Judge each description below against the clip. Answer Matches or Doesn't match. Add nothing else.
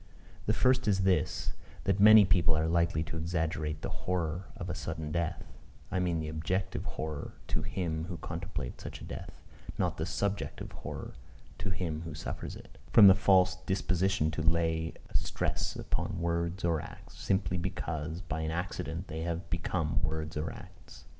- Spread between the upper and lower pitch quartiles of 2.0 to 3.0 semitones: Matches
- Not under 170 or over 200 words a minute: Matches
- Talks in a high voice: Doesn't match